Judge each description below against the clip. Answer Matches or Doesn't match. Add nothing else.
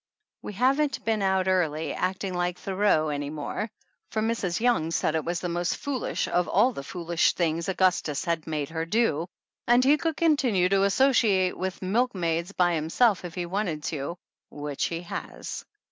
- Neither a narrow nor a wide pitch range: Matches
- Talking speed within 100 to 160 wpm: Doesn't match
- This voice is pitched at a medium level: Matches